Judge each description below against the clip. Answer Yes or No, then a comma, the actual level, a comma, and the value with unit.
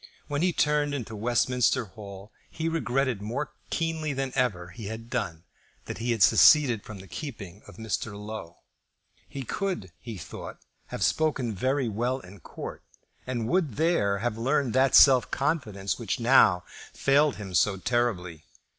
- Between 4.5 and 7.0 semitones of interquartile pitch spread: Yes, average, 5.2 semitones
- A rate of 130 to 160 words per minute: Yes, average, 155 wpm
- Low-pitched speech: Yes, low, 120 Hz